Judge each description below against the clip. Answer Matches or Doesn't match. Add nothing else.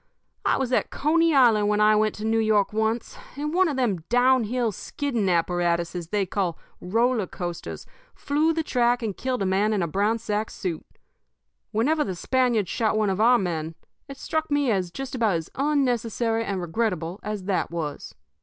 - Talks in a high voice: Matches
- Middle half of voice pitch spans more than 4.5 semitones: Matches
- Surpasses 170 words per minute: Matches